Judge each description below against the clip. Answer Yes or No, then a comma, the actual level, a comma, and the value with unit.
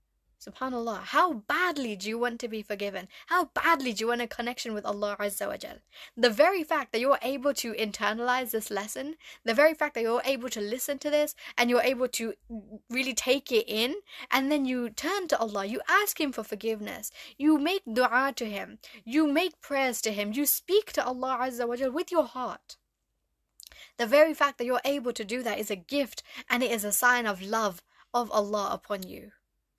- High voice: Yes, high, 245 Hz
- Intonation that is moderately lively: Yes, average, 4.7 semitones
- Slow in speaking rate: No, fast, 205 wpm